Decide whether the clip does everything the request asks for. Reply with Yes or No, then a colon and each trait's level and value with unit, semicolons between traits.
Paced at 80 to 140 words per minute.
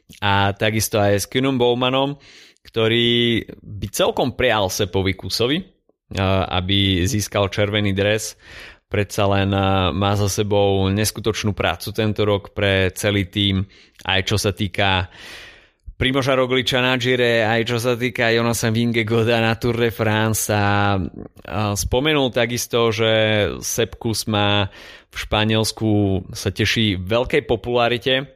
Yes: average, 125 wpm